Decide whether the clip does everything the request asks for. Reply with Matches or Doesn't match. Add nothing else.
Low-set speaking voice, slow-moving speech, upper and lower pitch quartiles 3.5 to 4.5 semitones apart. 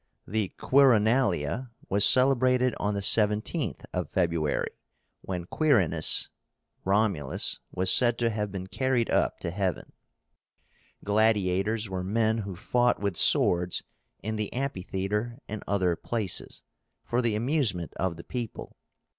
Matches